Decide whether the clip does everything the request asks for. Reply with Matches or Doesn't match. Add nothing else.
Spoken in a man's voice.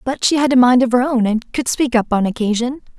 Doesn't match